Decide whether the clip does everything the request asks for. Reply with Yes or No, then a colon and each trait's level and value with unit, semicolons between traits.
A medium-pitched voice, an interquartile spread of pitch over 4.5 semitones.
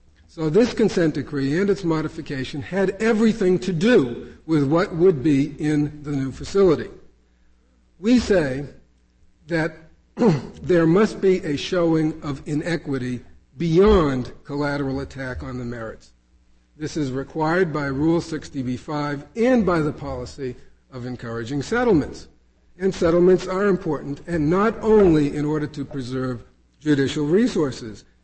Yes: medium, 150 Hz; average, 5.3 semitones